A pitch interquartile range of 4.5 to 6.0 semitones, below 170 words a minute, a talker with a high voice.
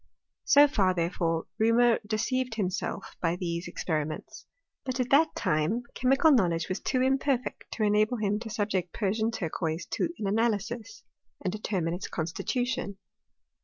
Yes: average, 5.3 semitones; average, 140 wpm; high, 210 Hz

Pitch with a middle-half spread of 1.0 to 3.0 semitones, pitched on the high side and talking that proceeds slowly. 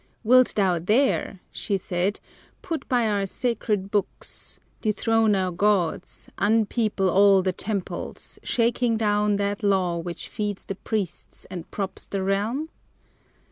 Yes: average, 2.7 semitones; high, 205 Hz; slow, 130 wpm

